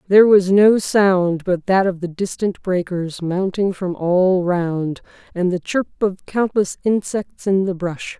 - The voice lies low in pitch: No, medium, 185 Hz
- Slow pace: No, average, 170 wpm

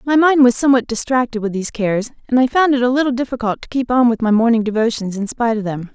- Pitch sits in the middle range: No, high, 240 Hz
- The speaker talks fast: Yes, fast, 265 wpm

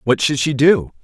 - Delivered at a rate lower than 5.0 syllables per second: Yes, 4.7 syllables/s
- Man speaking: Yes, male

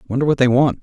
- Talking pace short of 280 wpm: No, fast, 290 wpm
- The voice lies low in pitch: Yes, low, 130 Hz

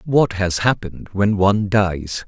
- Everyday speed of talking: Yes, average, 160 wpm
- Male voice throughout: Yes, male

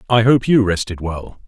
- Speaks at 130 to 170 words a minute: No, fast, 205 wpm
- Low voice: Yes, low, 105 Hz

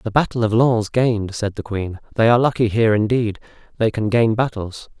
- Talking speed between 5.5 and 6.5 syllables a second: Yes, 5.6 syllables/s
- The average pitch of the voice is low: Yes, low, 110 Hz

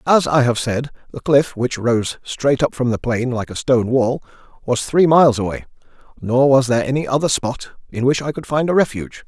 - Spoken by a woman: No, male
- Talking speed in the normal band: No, fast, 220 wpm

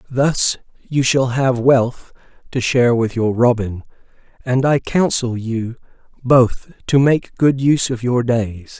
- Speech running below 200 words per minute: Yes, average, 150 wpm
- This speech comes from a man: Yes, male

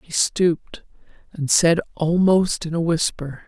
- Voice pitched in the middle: Yes, medium, 165 Hz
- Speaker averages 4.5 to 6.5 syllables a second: No, 4.0 syllables/s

